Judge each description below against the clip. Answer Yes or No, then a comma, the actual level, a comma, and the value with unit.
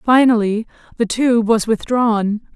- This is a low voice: No, high, 225 Hz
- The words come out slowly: Yes, slow, 115 wpm